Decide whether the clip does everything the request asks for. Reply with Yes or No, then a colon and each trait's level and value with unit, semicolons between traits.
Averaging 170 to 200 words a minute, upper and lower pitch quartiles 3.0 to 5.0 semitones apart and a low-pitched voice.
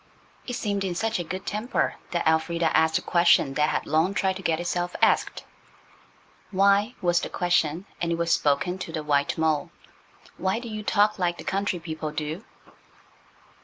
No: average, 175 wpm; average, 3.6 semitones; medium, 175 Hz